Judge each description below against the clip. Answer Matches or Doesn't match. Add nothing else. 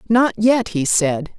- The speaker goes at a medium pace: Matches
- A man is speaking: Doesn't match